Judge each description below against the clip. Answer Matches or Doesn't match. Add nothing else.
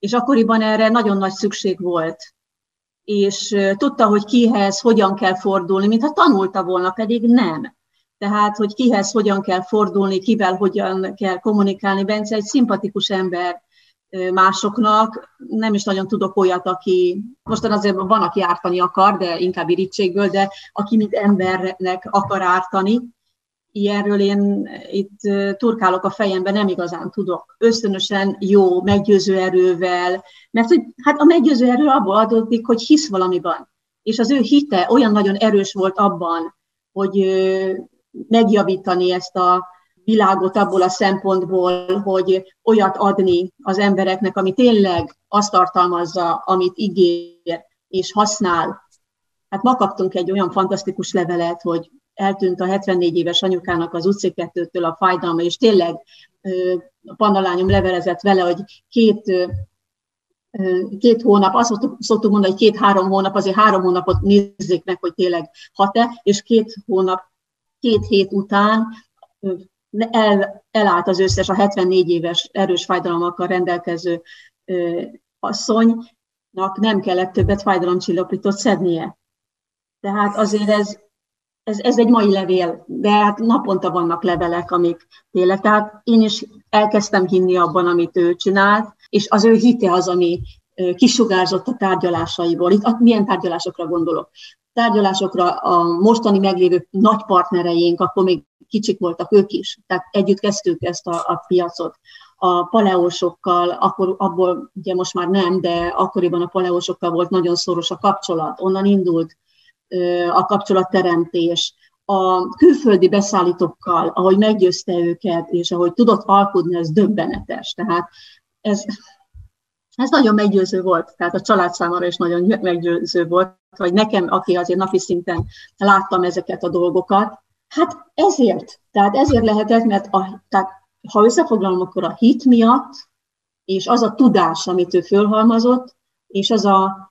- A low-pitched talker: Doesn't match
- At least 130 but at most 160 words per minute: Matches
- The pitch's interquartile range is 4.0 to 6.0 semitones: Doesn't match